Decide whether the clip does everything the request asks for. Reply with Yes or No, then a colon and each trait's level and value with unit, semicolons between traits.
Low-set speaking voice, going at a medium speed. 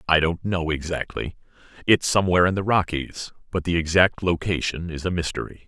Yes: very low, 85 Hz; average, 160 wpm